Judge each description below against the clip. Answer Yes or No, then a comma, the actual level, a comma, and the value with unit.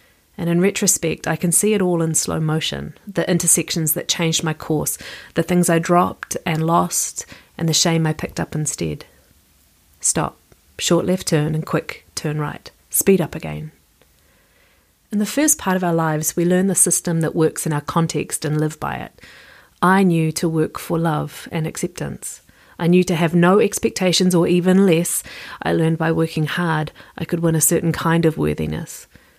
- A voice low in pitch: No, medium, 165 Hz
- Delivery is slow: No, average, 185 wpm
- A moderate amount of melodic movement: No, narrow, 2.3 semitones